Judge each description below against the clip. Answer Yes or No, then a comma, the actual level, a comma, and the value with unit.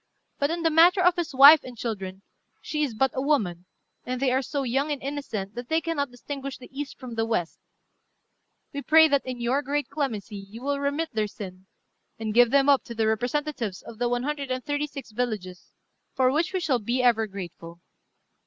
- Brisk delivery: Yes, fast, 210 wpm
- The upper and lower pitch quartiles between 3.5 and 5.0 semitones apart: Yes, average, 4.4 semitones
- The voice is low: No, very high, 255 Hz